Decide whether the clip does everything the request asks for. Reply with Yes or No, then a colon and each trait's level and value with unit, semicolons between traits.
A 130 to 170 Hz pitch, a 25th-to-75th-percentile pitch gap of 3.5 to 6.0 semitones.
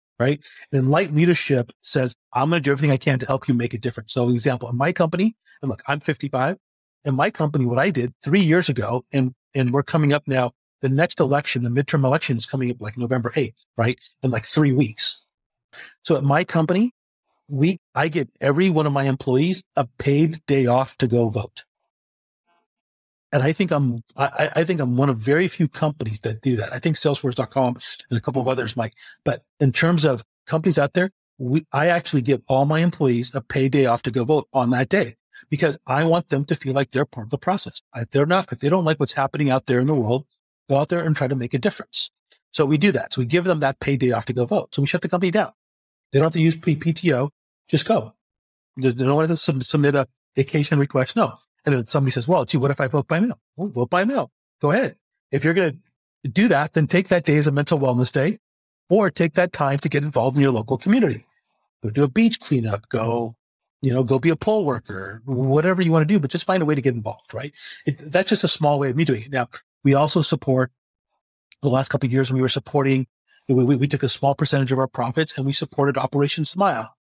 Yes: medium, 140 Hz; average, 3.8 semitones